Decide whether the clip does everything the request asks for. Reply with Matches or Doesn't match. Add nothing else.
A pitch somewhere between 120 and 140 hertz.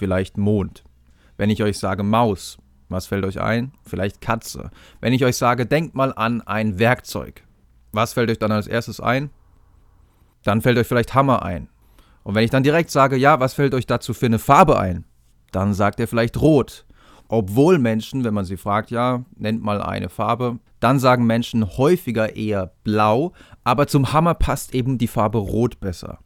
Doesn't match